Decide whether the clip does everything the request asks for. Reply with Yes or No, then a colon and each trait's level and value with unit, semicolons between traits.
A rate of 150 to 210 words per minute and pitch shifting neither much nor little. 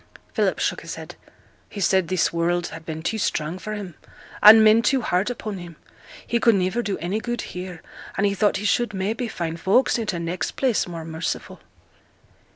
Yes: average, 195 wpm; average, 4.1 semitones